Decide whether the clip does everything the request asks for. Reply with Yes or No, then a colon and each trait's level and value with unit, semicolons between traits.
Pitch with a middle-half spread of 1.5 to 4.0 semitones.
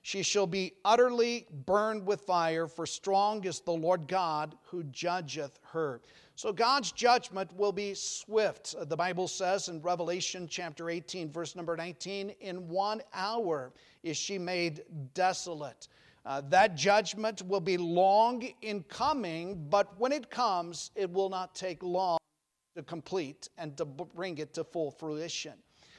Yes: average, 3.1 semitones